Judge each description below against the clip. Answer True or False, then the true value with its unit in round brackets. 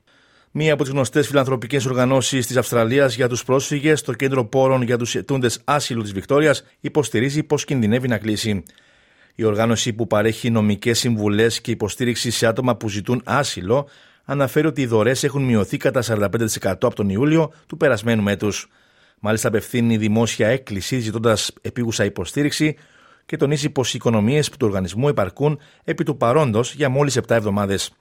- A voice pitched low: True (120 Hz)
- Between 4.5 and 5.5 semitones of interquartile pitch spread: False (3.9 semitones)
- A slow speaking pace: False (160 wpm)